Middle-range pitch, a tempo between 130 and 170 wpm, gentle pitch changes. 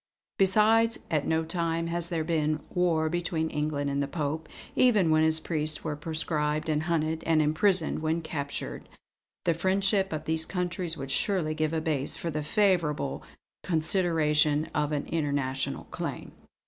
Yes: medium, 160 Hz; average, 155 wpm; narrow, 2.3 semitones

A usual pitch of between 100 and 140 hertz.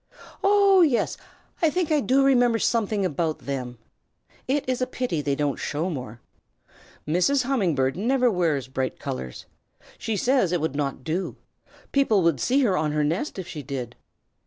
No: medium, 180 Hz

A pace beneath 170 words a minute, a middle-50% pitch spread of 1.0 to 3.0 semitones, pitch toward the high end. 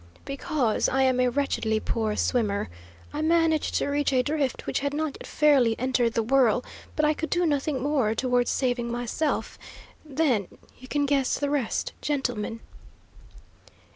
No: average, 160 wpm; average, 3.4 semitones; very high, 265 Hz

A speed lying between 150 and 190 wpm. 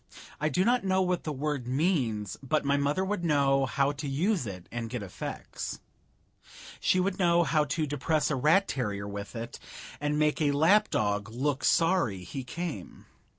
Yes: average, 180 wpm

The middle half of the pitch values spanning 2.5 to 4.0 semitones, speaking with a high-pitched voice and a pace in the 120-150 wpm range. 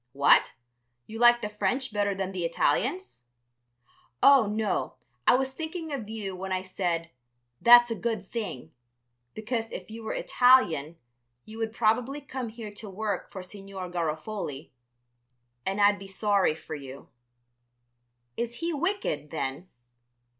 No: average, 4.6 semitones; high, 210 Hz; average, 140 wpm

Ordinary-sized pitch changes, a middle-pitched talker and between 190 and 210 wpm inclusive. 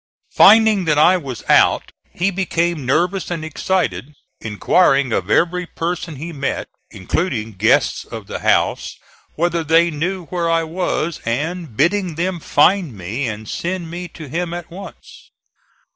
No: average, 4.0 semitones; medium, 165 Hz; average, 145 wpm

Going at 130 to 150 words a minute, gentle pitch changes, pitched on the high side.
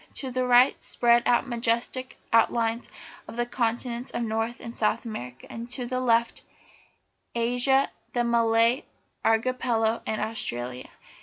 Yes: average, 140 wpm; narrow, 1.5 semitones; high, 235 Hz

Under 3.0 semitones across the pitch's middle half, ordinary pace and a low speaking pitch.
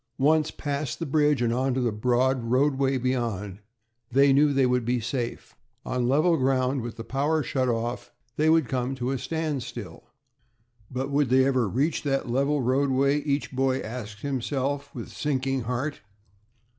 Yes: narrow, 2.4 semitones; average, 165 wpm; low, 130 Hz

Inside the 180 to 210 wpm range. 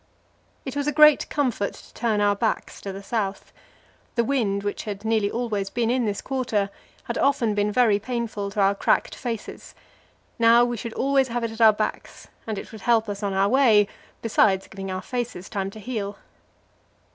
Yes: average, 190 wpm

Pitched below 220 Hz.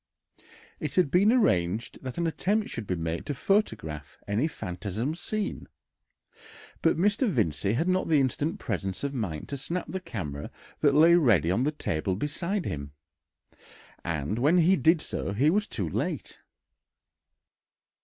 Yes: medium, 140 Hz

